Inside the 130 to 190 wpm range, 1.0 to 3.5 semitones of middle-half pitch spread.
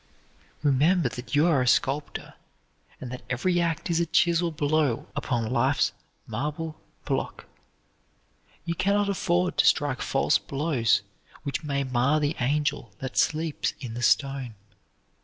No: average, 140 wpm; average, 4.3 semitones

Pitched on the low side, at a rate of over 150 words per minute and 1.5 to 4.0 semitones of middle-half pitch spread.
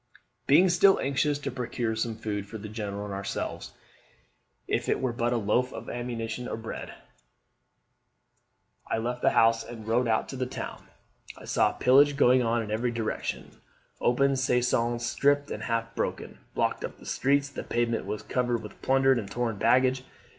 Yes: low, 120 Hz; average, 170 wpm; narrow, 2.5 semitones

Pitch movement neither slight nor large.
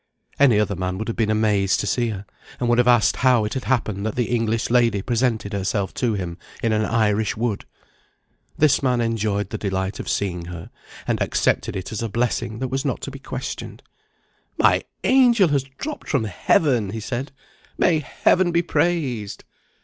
Yes: average, 4.0 semitones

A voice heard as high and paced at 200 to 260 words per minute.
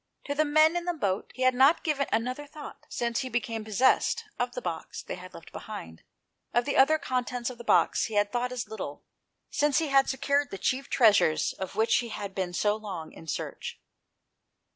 Yes: high, 245 Hz; fast, 205 wpm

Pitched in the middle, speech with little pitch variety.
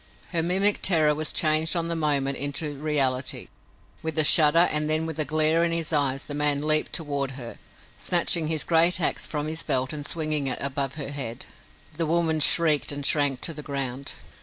Yes: medium, 150 Hz; narrow, 2.3 semitones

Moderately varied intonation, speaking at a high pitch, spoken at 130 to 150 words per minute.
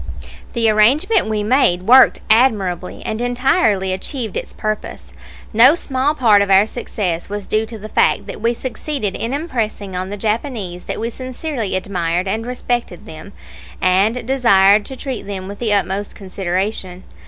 No: average, 4.2 semitones; high, 215 Hz; average, 160 wpm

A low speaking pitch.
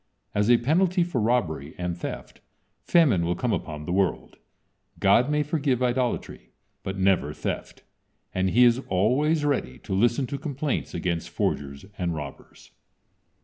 Yes: low, 115 Hz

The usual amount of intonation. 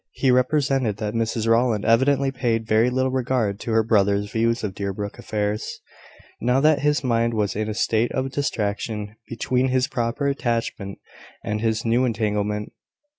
Yes: average, 3.3 semitones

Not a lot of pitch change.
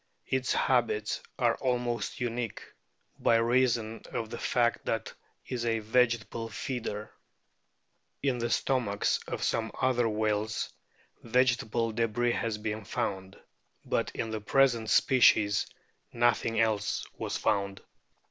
Yes: narrow, 2.0 semitones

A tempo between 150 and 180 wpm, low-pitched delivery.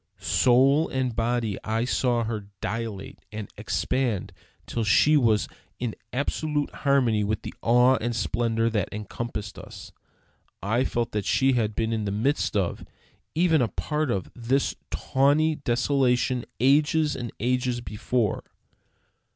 No: slow, 135 wpm; low, 120 Hz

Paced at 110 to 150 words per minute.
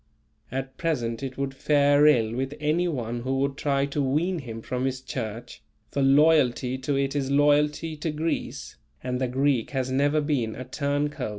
No: average, 185 wpm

